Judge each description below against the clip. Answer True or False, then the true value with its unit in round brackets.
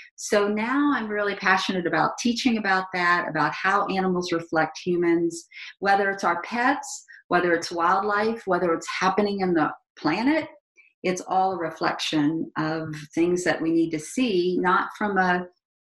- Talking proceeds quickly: False (155 wpm)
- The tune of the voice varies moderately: True (3.8 semitones)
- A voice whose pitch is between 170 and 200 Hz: True (185 Hz)